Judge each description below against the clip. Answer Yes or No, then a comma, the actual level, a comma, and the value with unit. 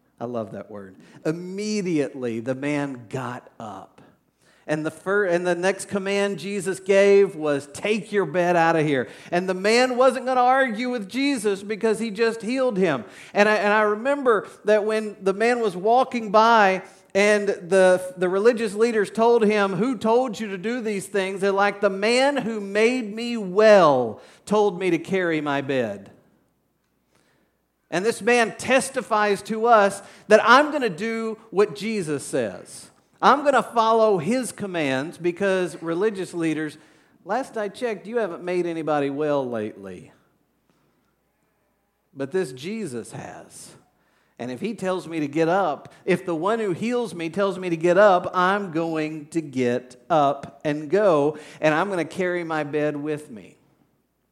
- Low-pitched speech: No, high, 195 Hz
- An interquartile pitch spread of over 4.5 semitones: Yes, average, 5.2 semitones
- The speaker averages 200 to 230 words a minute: No, average, 165 wpm